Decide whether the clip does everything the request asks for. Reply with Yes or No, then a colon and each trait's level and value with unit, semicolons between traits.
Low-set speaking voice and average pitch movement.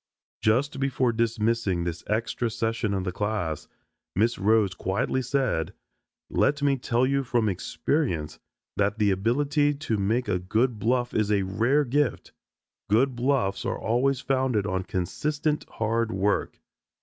Yes: low, 115 Hz; average, 4.6 semitones